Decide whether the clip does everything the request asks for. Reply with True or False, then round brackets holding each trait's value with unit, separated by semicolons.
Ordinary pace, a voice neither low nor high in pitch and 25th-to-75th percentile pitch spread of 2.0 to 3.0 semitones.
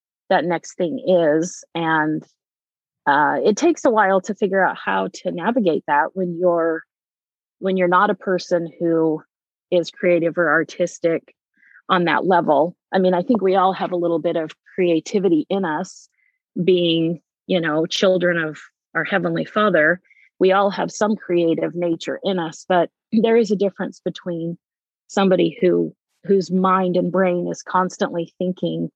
True (160 wpm; 180 Hz; 2.4 semitones)